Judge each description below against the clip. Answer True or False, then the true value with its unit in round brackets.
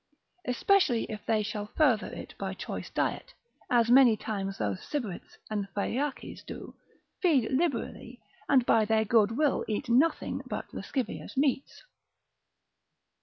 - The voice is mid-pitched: False (235 Hz)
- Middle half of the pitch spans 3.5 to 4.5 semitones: True (4.2 semitones)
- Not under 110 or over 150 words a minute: True (135 wpm)